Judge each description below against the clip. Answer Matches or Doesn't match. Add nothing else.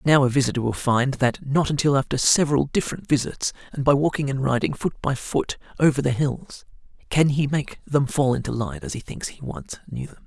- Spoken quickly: Matches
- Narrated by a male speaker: Matches